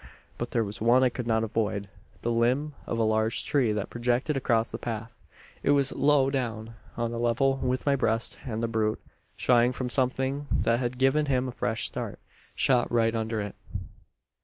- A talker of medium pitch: No, low, 120 Hz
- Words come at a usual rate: Yes, average, 190 wpm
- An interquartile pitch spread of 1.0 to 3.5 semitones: Yes, narrow, 2.6 semitones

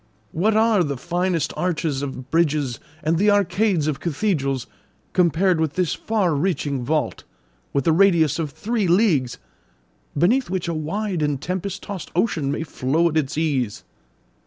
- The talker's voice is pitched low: No, medium, 165 Hz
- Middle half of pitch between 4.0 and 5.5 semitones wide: Yes, average, 4.6 semitones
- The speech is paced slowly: No, average, 155 wpm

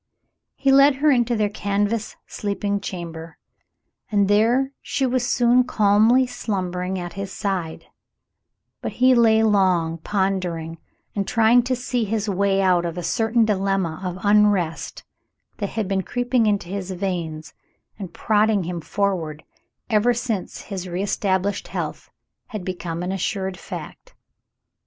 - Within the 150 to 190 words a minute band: No, average, 140 wpm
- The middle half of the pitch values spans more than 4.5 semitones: No, average, 3.6 semitones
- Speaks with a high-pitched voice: Yes, high, 200 Hz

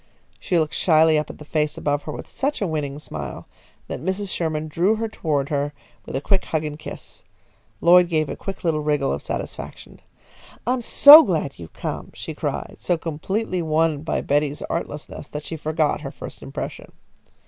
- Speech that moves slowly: No, average, 180 wpm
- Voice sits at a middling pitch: Yes, medium, 155 Hz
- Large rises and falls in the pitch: No, average, 3.0 semitones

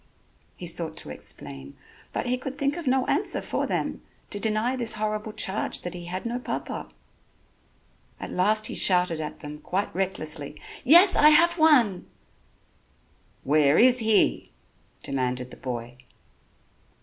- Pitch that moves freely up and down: Yes, wide, 8.4 semitones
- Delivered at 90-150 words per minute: Yes, average, 145 wpm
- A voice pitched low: No, high, 195 Hz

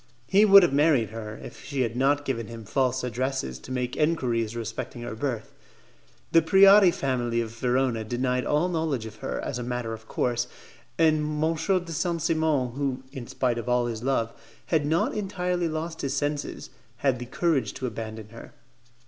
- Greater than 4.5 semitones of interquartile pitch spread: Yes, average, 5.1 semitones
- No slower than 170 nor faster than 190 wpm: Yes, average, 180 wpm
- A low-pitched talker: Yes, low, 130 Hz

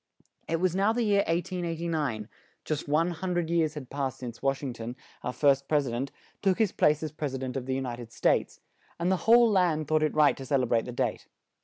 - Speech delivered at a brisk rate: Yes, fast, 250 wpm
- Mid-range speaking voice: Yes, medium, 150 Hz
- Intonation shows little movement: No, average, 4.6 semitones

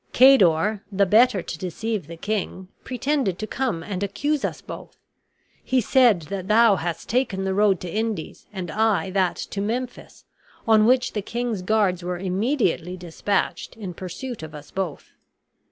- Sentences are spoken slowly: No, average, 165 wpm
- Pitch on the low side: No, high, 200 Hz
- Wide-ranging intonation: No, average, 4.0 semitones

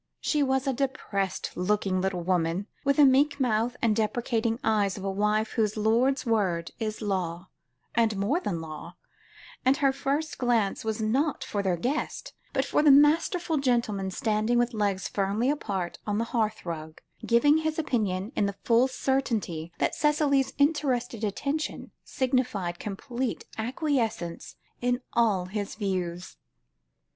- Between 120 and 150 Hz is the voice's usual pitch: No, high, 225 Hz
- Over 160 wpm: No, average, 150 wpm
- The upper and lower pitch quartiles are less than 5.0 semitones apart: No, average, 5.3 semitones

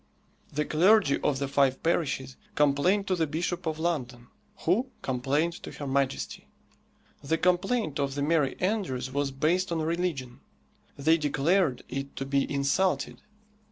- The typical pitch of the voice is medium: Yes, medium, 150 Hz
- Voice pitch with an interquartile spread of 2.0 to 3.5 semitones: No, average, 4.1 semitones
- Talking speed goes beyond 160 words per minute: No, average, 145 wpm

